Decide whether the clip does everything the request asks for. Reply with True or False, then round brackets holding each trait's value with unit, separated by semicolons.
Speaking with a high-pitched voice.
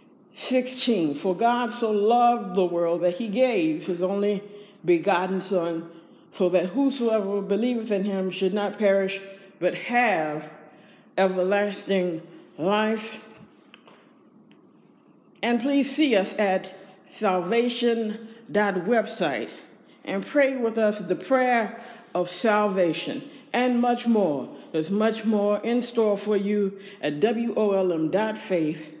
True (205 Hz)